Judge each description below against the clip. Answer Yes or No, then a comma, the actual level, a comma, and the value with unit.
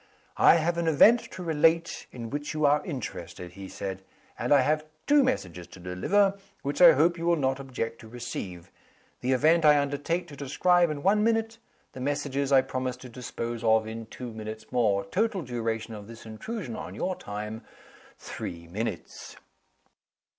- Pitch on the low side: Yes, low, 130 Hz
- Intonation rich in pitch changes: Yes, wide, 6.9 semitones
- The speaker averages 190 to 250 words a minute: No, average, 175 wpm